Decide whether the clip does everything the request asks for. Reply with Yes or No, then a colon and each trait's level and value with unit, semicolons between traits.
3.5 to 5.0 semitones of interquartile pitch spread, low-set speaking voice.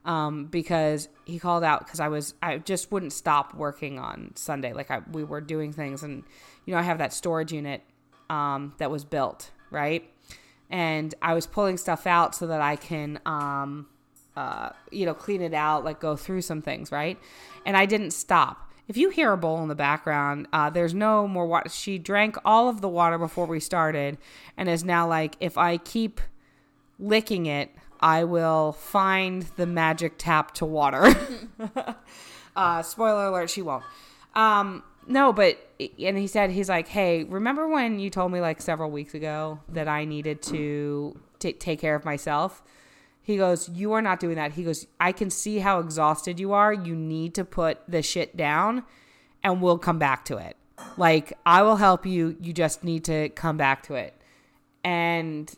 No: average, 3.9 semitones; medium, 165 Hz